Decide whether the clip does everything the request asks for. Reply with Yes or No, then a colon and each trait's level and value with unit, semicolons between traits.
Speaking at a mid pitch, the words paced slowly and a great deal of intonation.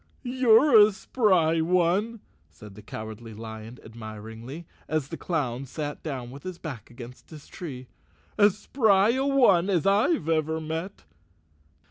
No: medium, 160 Hz; average, 150 wpm; wide, 8.7 semitones